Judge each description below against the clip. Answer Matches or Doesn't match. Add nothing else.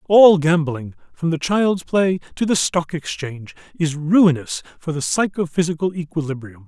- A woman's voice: Doesn't match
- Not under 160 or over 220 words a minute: Doesn't match